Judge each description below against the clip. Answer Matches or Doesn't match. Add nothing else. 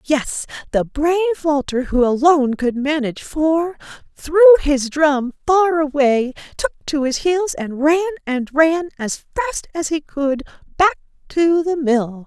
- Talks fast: Doesn't match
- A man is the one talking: Doesn't match